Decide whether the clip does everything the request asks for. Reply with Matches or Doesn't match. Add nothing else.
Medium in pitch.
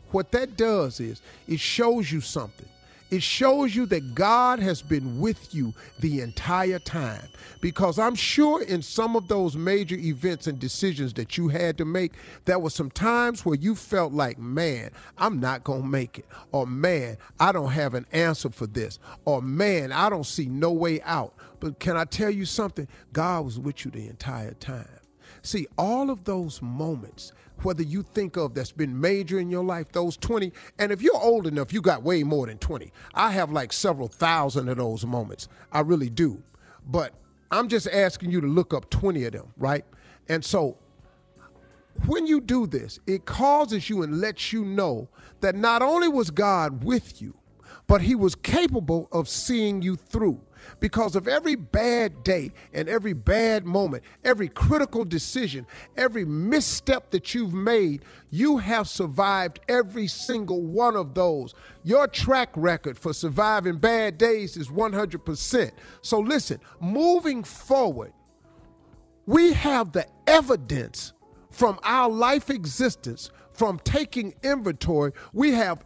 Matches